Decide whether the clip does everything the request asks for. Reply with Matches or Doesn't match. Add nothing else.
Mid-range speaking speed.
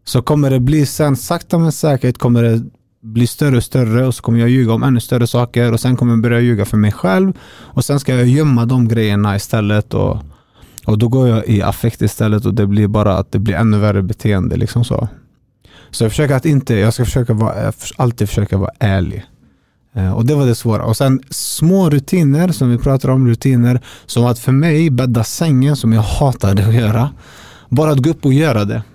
Doesn't match